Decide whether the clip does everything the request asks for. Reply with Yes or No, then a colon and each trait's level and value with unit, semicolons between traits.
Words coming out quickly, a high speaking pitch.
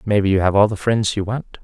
No: fast, 330 wpm; low, 105 Hz